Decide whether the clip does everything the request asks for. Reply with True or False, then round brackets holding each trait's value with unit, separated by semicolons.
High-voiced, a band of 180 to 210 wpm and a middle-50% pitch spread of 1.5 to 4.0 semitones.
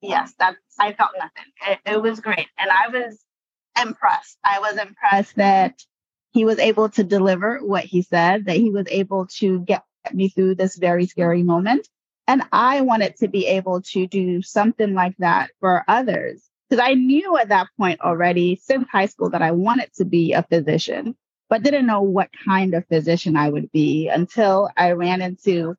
True (195 Hz; 190 wpm; 3.4 semitones)